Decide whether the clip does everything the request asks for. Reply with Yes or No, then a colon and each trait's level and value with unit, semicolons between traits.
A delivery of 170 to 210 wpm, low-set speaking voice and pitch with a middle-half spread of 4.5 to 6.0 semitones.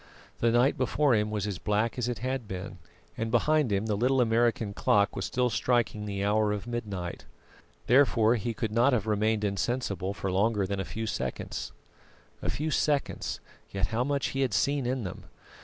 No: average, 190 wpm; low, 110 Hz; average, 3.4 semitones